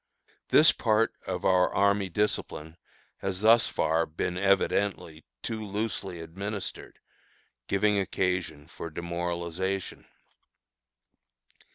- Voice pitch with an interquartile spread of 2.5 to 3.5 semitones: Yes, average, 2.9 semitones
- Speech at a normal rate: No, slow, 90 wpm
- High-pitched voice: No, very low, 95 Hz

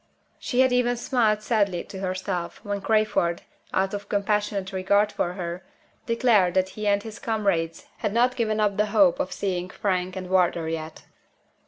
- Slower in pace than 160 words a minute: No, average, 170 wpm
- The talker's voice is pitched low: No, high, 200 Hz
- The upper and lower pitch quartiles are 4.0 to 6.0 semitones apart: No, average, 2.8 semitones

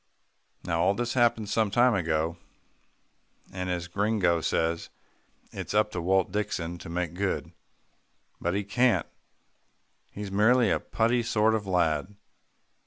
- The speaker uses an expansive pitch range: No, average, 4.1 semitones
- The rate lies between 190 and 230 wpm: No, slow, 135 wpm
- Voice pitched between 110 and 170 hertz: No, low, 100 Hz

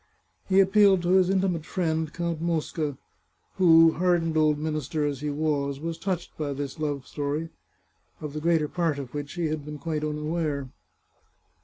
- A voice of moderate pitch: Yes, medium, 155 Hz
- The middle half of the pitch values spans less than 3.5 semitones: Yes, narrow, 2.5 semitones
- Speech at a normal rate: Yes, average, 170 wpm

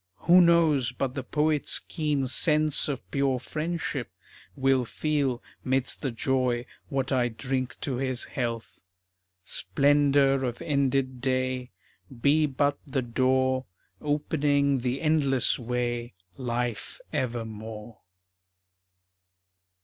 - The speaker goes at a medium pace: No, slow, 105 wpm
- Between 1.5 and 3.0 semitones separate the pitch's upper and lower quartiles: Yes, narrow, 2.6 semitones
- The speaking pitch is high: No, low, 130 Hz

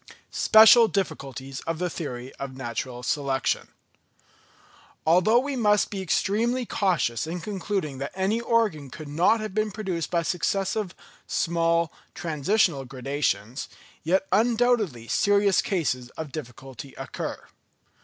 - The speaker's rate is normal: No, slow, 120 wpm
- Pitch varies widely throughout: Yes, wide, 7.2 semitones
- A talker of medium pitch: Yes, medium, 170 Hz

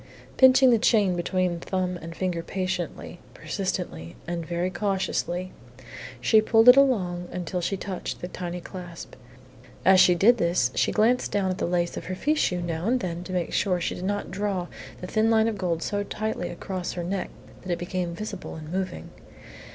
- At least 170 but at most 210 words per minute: Yes, average, 190 wpm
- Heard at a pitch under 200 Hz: Yes, medium, 185 Hz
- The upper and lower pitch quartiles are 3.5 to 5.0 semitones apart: No, average, 2.7 semitones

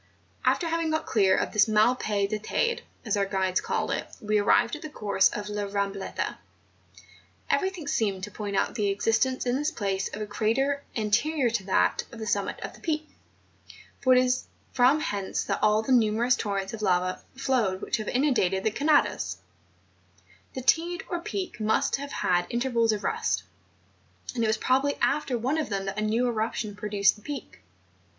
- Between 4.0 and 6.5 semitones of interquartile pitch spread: Yes, average, 4.8 semitones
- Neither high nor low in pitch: No, high, 220 Hz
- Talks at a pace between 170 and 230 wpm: Yes, average, 190 wpm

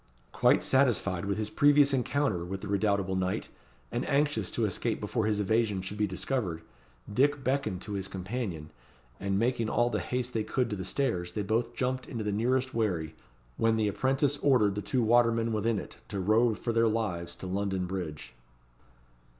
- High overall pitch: No, low, 110 Hz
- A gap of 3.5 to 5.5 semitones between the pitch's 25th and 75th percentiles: Yes, average, 4.3 semitones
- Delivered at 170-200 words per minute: Yes, average, 185 wpm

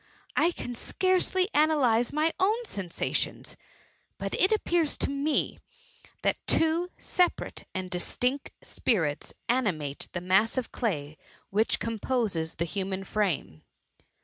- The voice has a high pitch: Yes, high, 230 Hz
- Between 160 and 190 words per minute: No, slow, 135 wpm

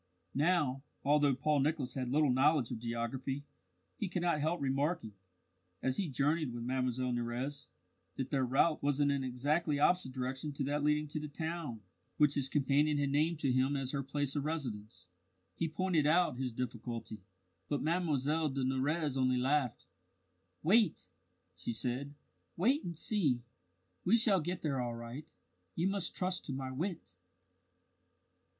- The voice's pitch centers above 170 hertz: No, medium, 140 Hz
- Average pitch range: Yes, average, 3.4 semitones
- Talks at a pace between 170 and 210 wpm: No, average, 160 wpm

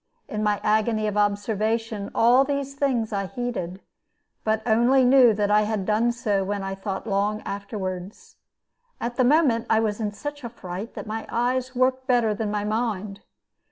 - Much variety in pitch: No, average, 2.9 semitones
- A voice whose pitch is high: Yes, high, 220 Hz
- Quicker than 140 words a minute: Yes, average, 175 wpm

